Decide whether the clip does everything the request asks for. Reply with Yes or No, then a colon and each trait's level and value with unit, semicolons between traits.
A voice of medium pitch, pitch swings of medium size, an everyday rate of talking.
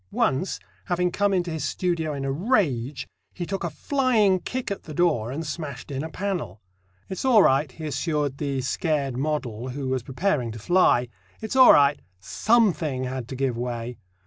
No: medium, 150 Hz; wide, 5.7 semitones; average, 180 wpm